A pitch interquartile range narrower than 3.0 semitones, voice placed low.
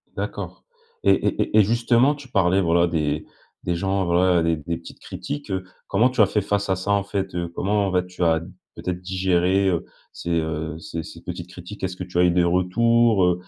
Yes: narrow, 2.6 semitones; very low, 90 Hz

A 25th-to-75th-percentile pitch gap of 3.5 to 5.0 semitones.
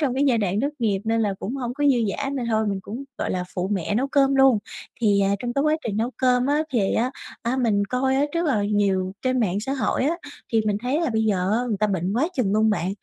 Yes: average, 4.7 semitones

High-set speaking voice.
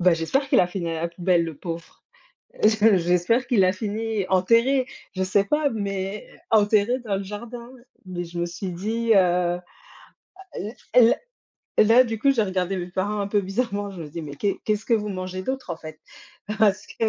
Yes: high, 195 Hz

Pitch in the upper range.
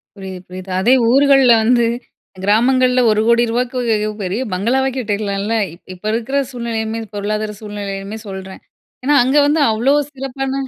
Yes: high, 225 Hz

